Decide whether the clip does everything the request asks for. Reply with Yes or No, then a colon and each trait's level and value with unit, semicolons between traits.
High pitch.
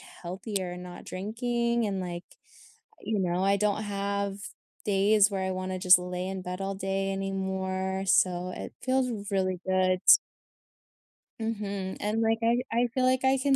Yes: high, 195 Hz